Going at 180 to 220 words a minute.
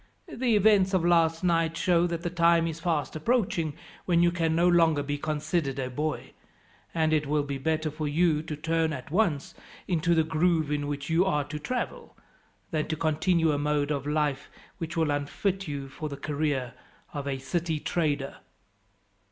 Yes: average, 185 wpm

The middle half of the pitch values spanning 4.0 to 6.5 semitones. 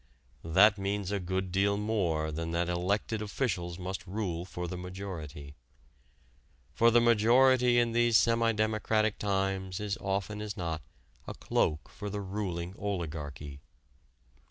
No: average, 3.6 semitones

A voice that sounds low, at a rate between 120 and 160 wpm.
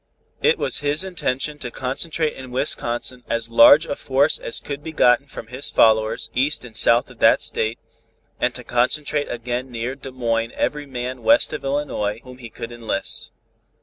No: low, 125 Hz; average, 180 wpm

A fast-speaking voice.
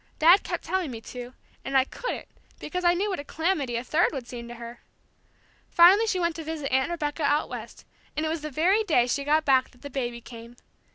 Yes: fast, 230 wpm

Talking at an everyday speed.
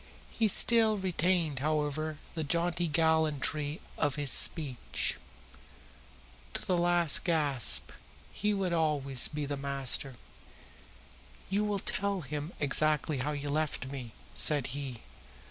No: slow, 125 wpm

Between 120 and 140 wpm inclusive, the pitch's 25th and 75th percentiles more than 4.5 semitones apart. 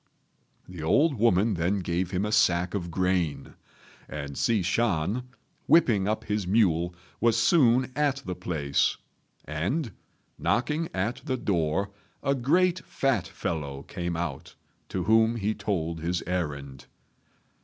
Yes: slow, 135 wpm; wide, 5.6 semitones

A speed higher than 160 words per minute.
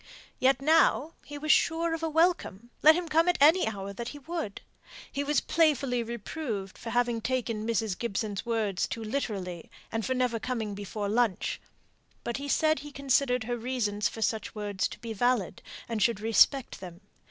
Yes: average, 175 wpm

